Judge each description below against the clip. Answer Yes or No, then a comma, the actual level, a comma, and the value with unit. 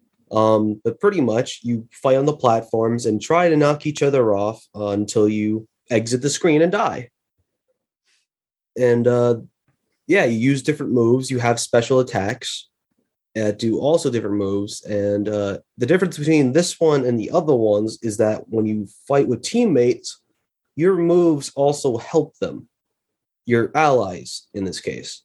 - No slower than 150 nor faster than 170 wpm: Yes, average, 160 wpm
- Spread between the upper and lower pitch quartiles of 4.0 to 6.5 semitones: Yes, wide, 5.6 semitones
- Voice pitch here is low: Yes, low, 120 Hz